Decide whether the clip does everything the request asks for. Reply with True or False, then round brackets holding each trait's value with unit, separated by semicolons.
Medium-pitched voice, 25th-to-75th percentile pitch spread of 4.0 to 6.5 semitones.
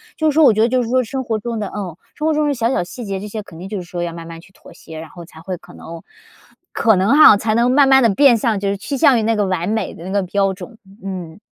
False (210 Hz; 4.6 semitones)